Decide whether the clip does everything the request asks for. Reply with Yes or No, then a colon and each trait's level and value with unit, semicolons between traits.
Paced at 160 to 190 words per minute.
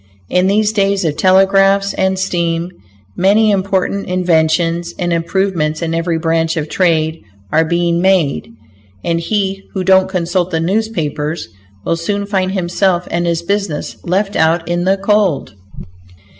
No: average, 145 wpm